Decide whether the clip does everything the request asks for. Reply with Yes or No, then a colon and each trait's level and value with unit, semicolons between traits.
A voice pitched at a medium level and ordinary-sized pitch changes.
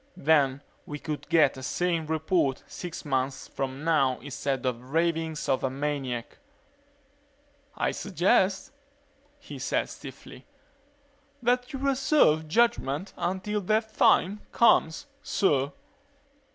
No: medium, 160 Hz; wide, 5.8 semitones